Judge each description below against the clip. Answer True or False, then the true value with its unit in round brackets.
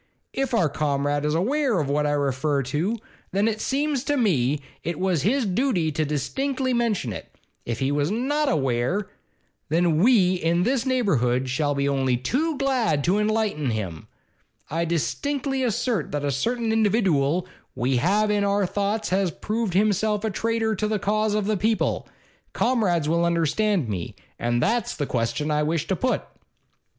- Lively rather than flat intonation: True (7.4 semitones)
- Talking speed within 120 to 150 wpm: False (170 wpm)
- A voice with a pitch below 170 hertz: False (185 Hz)